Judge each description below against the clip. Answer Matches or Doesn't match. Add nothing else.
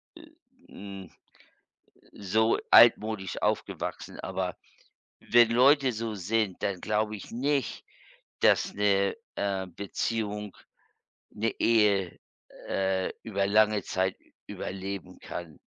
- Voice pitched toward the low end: Matches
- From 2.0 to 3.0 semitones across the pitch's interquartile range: Matches